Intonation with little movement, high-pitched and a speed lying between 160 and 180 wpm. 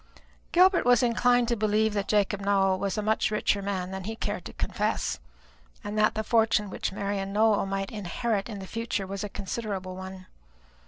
No: narrow, 2.2 semitones; high, 205 Hz; average, 190 wpm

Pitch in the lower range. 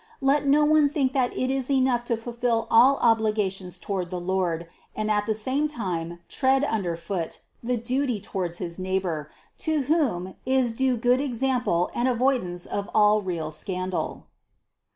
No: high, 225 Hz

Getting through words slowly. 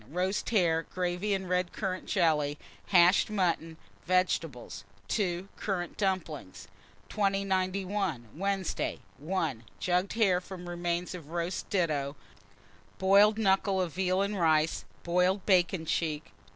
Yes: slow, 115 wpm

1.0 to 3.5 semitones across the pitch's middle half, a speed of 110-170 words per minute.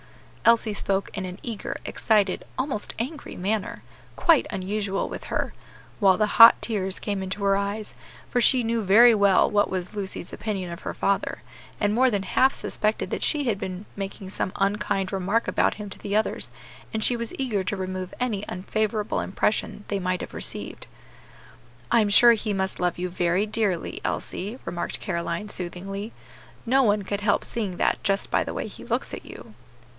No: narrow, 2.6 semitones; average, 180 wpm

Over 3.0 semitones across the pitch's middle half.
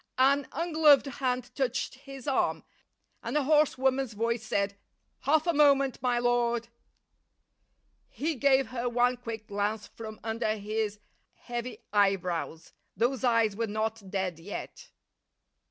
Yes: average, 3.8 semitones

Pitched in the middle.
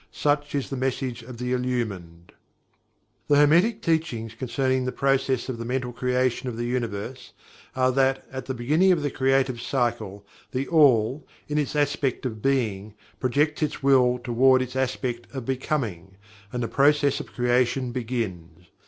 No: low, 130 Hz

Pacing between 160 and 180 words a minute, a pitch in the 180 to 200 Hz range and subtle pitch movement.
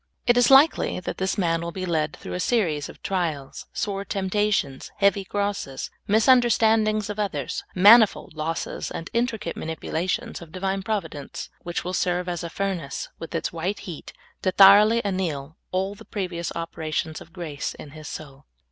No: average, 165 wpm; medium, 185 Hz; average, 4.1 semitones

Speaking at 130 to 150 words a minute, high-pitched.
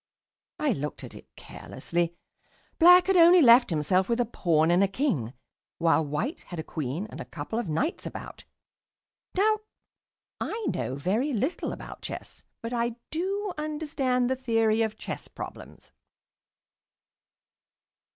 Yes: average, 140 wpm; high, 235 Hz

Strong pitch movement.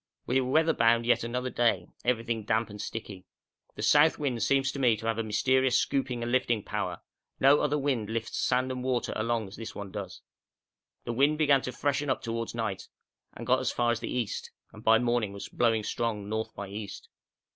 No: average, 2.9 semitones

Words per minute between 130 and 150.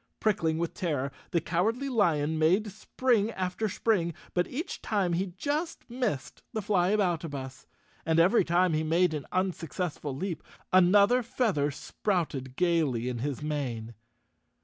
Yes: average, 140 wpm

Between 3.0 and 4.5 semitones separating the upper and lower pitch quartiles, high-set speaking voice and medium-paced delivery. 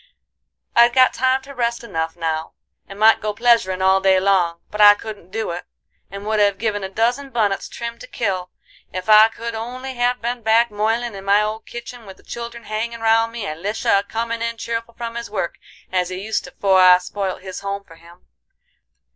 No: average, 3.4 semitones; high, 215 Hz; fast, 210 wpm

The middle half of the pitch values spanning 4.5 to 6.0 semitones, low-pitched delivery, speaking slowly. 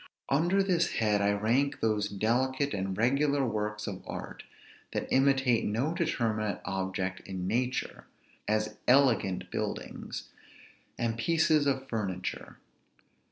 Yes: average, 4.9 semitones; low, 115 Hz; slow, 115 wpm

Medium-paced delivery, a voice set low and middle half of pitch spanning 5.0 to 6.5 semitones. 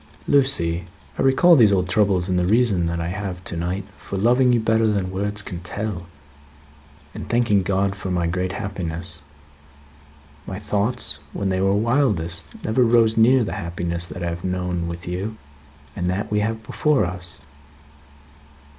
No: average, 165 wpm; very low, 95 Hz; average, 4.1 semitones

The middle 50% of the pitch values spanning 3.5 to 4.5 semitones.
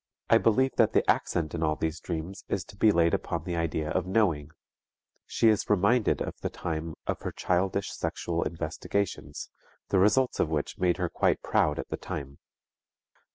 Yes: average, 4.0 semitones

